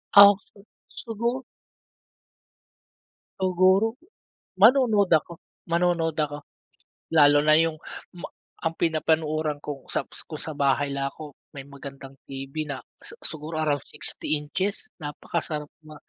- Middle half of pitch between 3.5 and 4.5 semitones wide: Yes, average, 4.1 semitones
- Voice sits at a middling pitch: Yes, medium, 155 Hz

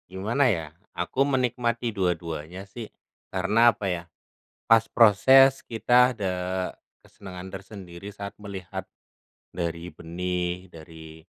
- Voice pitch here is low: Yes, very low, 95 Hz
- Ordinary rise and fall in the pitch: Yes, average, 4.8 semitones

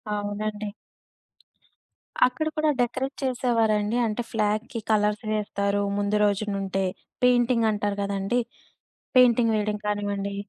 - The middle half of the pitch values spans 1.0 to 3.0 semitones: Yes, narrow, 2.6 semitones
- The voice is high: Yes, high, 210 Hz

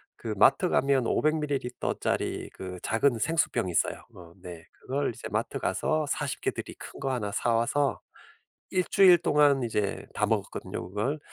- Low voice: Yes, low, 130 Hz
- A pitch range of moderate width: No, wide, 5.9 semitones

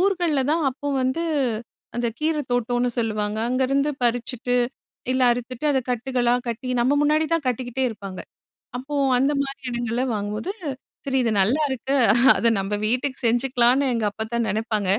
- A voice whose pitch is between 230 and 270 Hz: Yes, very high, 250 Hz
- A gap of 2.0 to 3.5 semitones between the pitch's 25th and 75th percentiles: Yes, average, 3.2 semitones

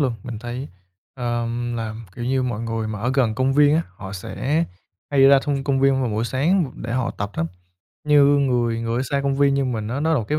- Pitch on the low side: Yes, low, 125 Hz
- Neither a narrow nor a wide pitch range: Yes, average, 3.3 semitones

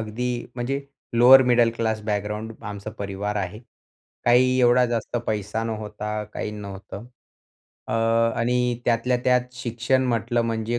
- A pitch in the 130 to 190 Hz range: No, low, 115 Hz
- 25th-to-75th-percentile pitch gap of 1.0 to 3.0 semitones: Yes, narrow, 2.6 semitones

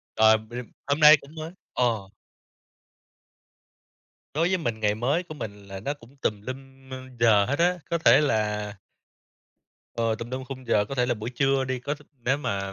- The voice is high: No, low, 125 Hz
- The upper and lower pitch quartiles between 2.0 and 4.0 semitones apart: No, average, 4.7 semitones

